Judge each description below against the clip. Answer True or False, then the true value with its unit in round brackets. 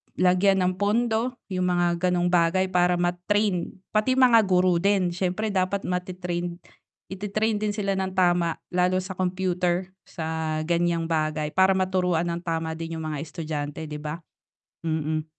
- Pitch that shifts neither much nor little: False (2.2 semitones)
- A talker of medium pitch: True (180 Hz)